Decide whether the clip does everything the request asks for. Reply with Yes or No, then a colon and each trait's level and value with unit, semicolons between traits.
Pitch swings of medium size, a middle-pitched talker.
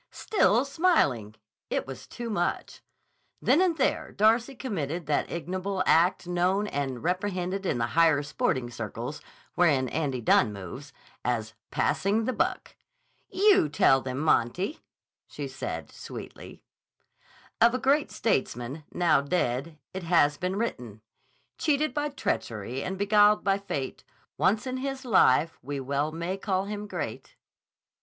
No: wide, 7.6 semitones; medium, 175 Hz